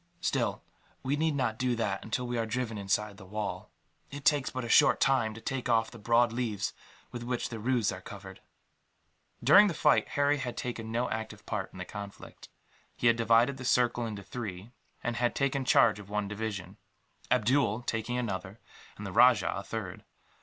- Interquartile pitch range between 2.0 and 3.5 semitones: Yes, average, 3.1 semitones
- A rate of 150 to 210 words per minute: Yes, average, 190 wpm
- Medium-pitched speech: No, low, 115 Hz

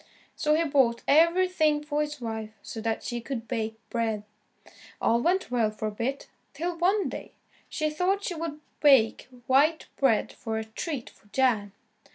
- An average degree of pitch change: No, wide, 5.9 semitones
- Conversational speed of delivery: Yes, average, 170 wpm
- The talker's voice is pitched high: Yes, very high, 270 Hz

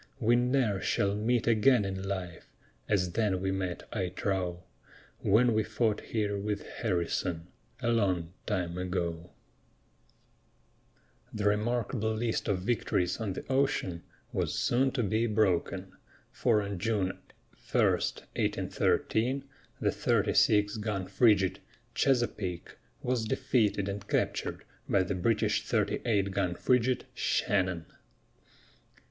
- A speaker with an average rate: No, slow, 120 wpm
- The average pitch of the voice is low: Yes, low, 105 Hz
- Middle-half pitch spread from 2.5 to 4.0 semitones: Yes, average, 3.6 semitones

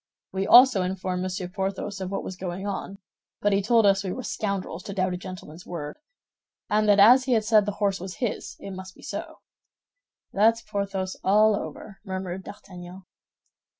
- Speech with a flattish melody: Yes, narrow, 1.9 semitones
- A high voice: Yes, high, 195 Hz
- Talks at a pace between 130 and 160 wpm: No, average, 185 wpm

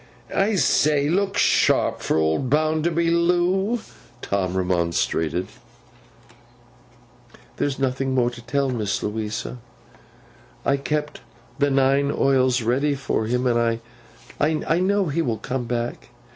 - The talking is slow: Yes, slow, 115 wpm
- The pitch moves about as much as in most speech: Yes, average, 5.0 semitones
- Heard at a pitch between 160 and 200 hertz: No, low, 135 Hz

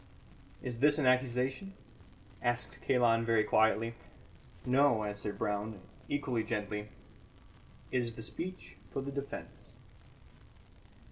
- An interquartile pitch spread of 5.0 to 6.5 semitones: No, average, 3.5 semitones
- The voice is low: Yes, low, 120 Hz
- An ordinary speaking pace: No, slow, 110 wpm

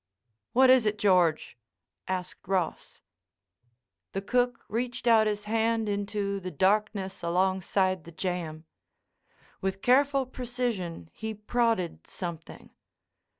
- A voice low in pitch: No, high, 200 Hz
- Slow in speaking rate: Yes, slow, 105 wpm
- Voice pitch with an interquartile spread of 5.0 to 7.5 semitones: No, average, 3.9 semitones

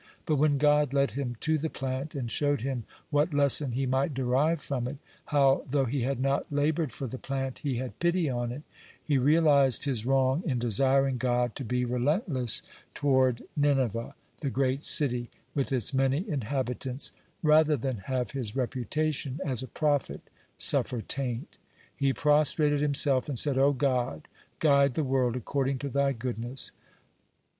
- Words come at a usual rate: Yes, average, 165 wpm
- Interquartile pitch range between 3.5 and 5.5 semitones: No, narrow, 2.4 semitones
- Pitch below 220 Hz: Yes, low, 135 Hz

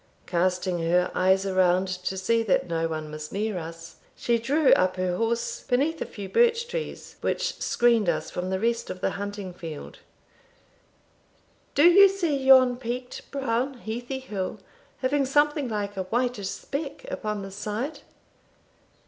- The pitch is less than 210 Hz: No, high, 215 Hz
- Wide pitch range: Yes, wide, 6.3 semitones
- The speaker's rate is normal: Yes, average, 155 wpm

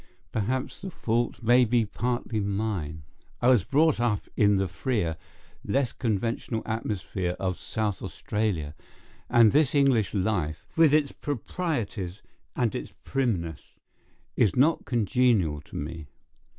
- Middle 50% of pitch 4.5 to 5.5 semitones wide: Yes, average, 5.0 semitones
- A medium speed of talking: No, slow, 125 wpm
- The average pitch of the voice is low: Yes, low, 110 Hz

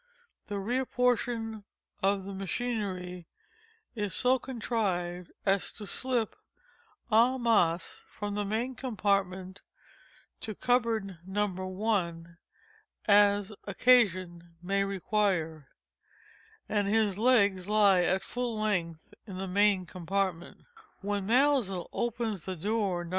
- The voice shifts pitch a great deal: No, average, 3.4 semitones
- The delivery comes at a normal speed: No, slow, 115 wpm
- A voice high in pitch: Yes, high, 200 Hz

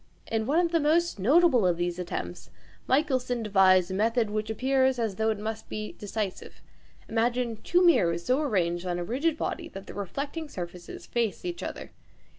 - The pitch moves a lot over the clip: Yes, wide, 6.1 semitones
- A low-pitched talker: No, high, 225 Hz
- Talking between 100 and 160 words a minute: No, average, 180 wpm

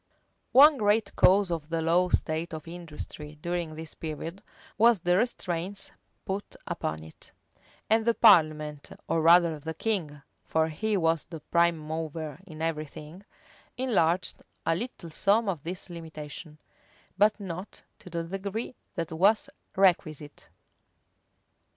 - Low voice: No, medium, 170 Hz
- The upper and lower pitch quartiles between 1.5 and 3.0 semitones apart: No, average, 3.7 semitones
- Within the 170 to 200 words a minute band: No, average, 140 wpm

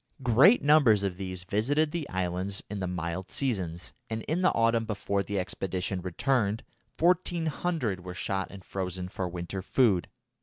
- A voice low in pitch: Yes, low, 100 Hz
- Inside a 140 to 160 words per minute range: Yes, average, 155 wpm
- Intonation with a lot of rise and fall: Yes, wide, 6.2 semitones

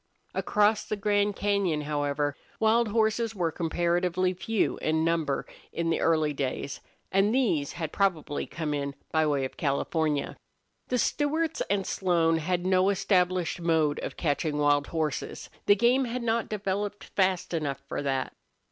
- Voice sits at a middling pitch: Yes, medium, 175 Hz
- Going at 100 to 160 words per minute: Yes, average, 150 wpm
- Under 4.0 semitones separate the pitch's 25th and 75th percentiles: No, average, 5.2 semitones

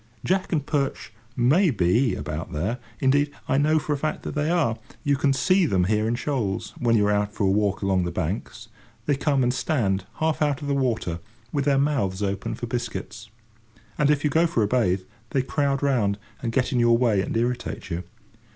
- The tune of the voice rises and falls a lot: Yes, wide, 5.8 semitones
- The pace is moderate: No, fast, 215 wpm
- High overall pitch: No, low, 125 Hz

